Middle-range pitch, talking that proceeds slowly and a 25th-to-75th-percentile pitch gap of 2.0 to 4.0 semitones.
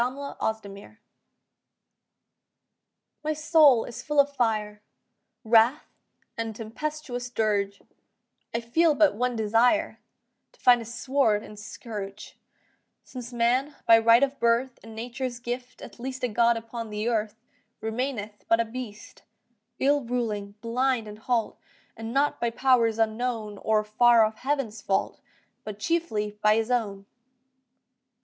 No: high, 230 Hz; slow, 130 wpm; average, 2.8 semitones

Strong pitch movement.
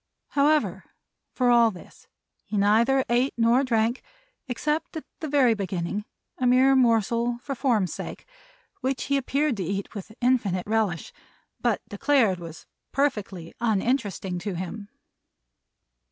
No: average, 4.7 semitones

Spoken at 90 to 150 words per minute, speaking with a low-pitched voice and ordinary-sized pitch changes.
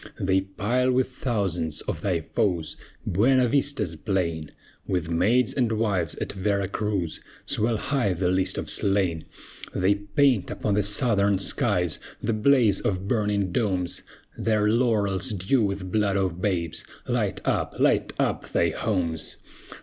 Yes: average, 140 wpm; low, 100 Hz; average, 3.3 semitones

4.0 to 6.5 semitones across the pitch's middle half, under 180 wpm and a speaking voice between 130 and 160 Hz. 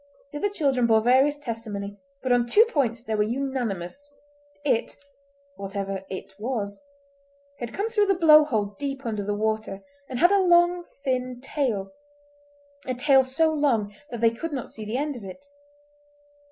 No: average, 4.9 semitones; average, 160 wpm; very high, 260 Hz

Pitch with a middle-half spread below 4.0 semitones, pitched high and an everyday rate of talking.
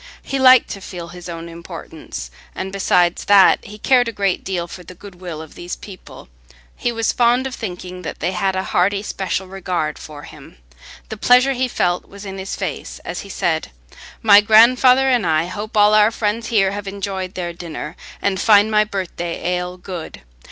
Yes: average, 3.2 semitones; high, 195 Hz; average, 195 wpm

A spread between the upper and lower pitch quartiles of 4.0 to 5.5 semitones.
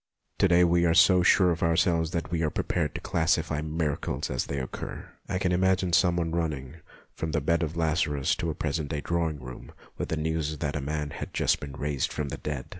No: narrow, 2.6 semitones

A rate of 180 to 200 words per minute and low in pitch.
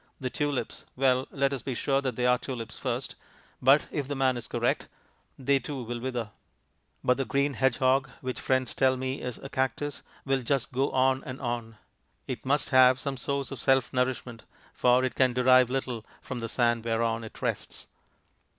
Yes: average, 185 wpm; low, 130 Hz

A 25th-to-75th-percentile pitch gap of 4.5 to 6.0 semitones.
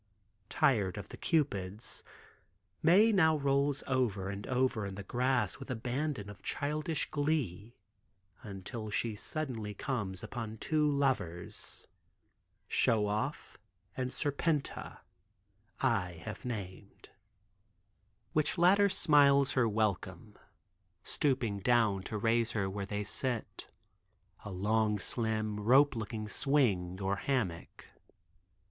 Yes: wide, 5.4 semitones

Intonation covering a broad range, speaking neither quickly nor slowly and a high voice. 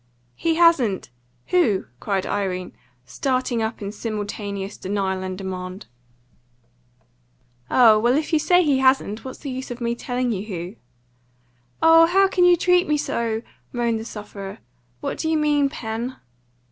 Yes: wide, 6.6 semitones; average, 150 wpm; high, 235 Hz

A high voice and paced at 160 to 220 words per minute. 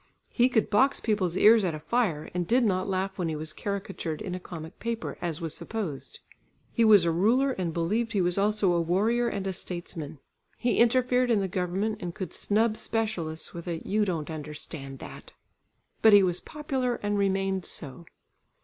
Yes: high, 195 Hz; average, 190 wpm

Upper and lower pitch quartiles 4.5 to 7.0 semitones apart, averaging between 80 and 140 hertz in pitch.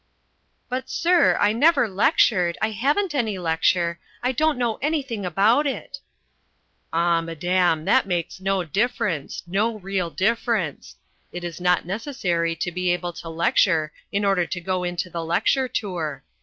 No: average, 5.2 semitones; medium, 185 Hz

